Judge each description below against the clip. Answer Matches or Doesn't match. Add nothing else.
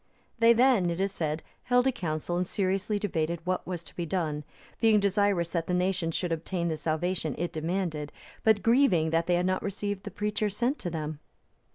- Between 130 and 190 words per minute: Doesn't match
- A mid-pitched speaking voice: Matches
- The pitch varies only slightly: Doesn't match